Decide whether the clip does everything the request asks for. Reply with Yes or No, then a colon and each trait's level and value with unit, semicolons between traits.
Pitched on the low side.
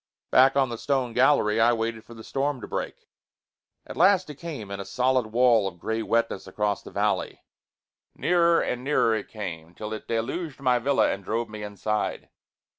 Yes: low, 115 Hz